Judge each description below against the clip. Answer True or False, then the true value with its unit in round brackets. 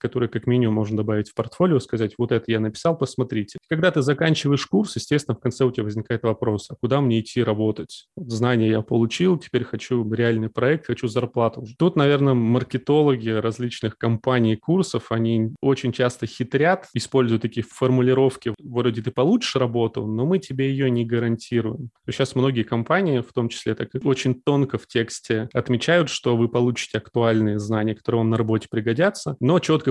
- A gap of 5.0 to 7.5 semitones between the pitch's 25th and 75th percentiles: False (2.8 semitones)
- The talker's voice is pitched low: True (120 Hz)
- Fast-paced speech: True (175 wpm)